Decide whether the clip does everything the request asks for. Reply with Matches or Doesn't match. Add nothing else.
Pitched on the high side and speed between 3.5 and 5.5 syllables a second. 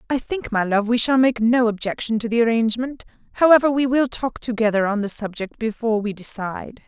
Doesn't match